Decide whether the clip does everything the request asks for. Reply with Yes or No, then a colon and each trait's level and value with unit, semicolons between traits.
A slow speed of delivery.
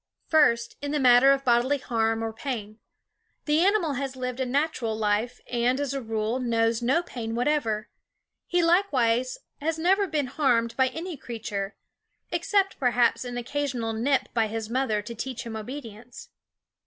No: average, 165 wpm